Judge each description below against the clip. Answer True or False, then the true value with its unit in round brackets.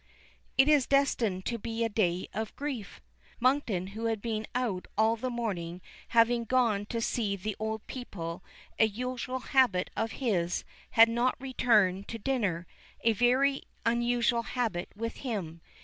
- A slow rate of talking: False (150 wpm)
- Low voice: False (230 Hz)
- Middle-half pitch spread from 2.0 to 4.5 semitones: True (3.5 semitones)